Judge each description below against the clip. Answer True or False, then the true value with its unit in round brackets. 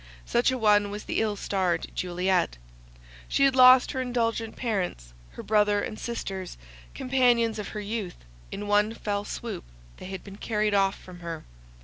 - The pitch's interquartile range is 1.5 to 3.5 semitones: True (3.1 semitones)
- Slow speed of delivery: False (165 wpm)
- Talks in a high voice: True (210 Hz)